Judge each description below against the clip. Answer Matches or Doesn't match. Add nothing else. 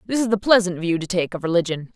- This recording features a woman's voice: Matches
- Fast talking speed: Matches